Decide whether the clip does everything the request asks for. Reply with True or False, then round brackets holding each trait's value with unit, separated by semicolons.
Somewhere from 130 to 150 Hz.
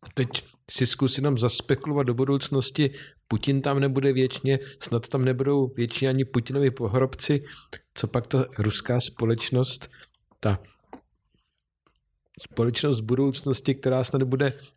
True (135 Hz)